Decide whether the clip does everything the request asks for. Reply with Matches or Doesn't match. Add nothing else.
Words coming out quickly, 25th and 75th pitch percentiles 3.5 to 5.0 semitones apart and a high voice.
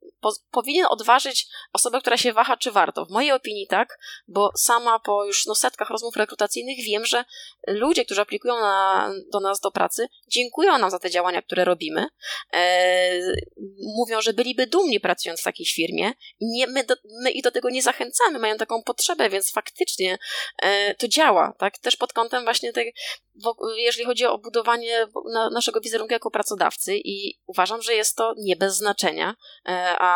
Matches